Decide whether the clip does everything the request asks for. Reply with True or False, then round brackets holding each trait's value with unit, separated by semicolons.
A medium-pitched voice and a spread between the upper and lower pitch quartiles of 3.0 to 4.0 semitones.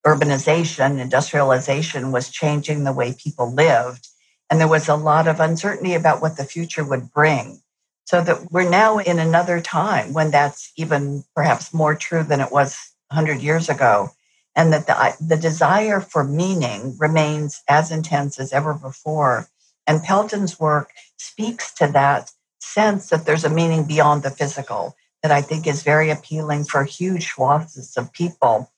False (155 Hz; 2.4 semitones)